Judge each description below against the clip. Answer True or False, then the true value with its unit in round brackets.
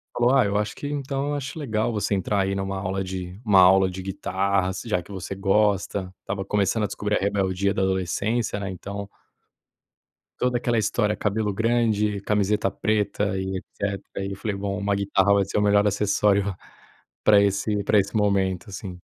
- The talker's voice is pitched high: False (100 Hz)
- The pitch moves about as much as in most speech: False (1.6 semitones)